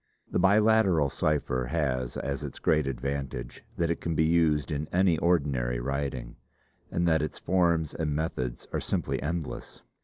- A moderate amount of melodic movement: Yes, average, 3.8 semitones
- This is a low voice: Yes, very low, 75 Hz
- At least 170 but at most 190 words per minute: No, average, 155 wpm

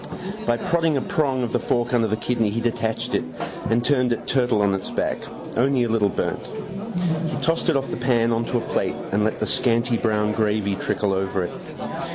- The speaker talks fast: Yes, fast, 210 wpm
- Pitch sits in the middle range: No, low, 115 Hz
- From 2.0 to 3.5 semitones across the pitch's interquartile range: Yes, average, 2.8 semitones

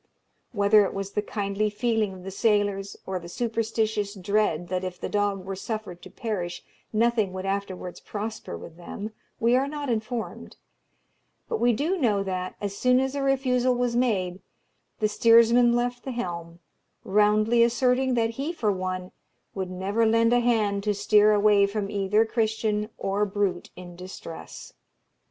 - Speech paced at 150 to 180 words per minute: Yes, average, 165 wpm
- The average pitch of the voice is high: Yes, high, 210 Hz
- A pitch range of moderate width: Yes, average, 3.3 semitones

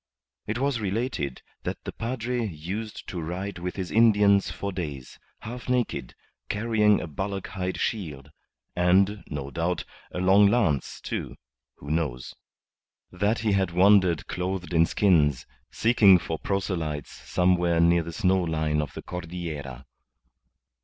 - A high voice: No, very low, 90 Hz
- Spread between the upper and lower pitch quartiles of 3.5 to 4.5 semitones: Yes, average, 4.0 semitones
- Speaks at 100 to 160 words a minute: Yes, average, 140 wpm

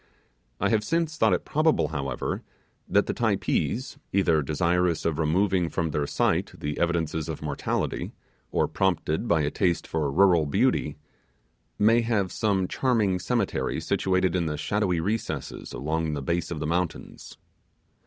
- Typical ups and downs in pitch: Yes, average, 4.4 semitones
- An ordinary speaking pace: Yes, average, 150 wpm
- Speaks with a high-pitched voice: No, very low, 85 Hz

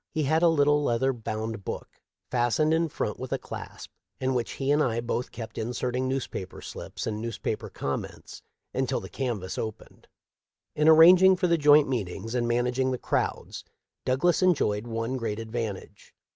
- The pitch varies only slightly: No, average, 4.5 semitones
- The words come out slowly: No, average, 165 wpm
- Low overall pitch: Yes, low, 125 Hz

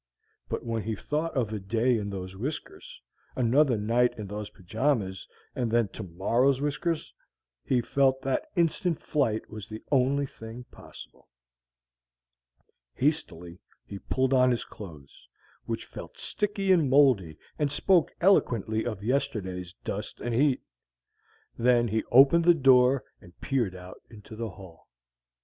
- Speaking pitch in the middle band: No, low, 120 Hz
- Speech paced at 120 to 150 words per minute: Yes, average, 140 wpm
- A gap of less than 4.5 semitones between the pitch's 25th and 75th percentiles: No, average, 5.1 semitones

